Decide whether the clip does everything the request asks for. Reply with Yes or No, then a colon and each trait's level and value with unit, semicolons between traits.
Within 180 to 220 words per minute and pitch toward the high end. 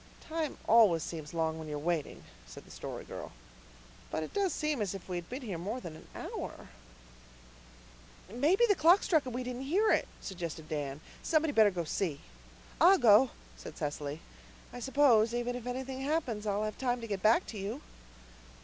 Yes: average, 190 wpm; high, 225 Hz